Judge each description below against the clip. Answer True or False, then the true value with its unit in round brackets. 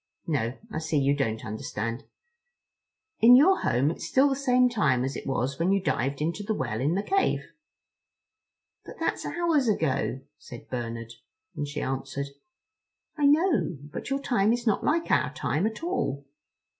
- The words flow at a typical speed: True (170 wpm)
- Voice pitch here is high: False (160 Hz)